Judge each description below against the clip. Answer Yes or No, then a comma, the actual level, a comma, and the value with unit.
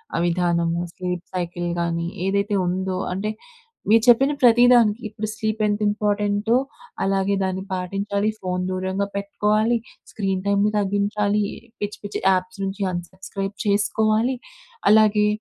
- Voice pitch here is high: Yes, high, 200 Hz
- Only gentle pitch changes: Yes, narrow, 2.1 semitones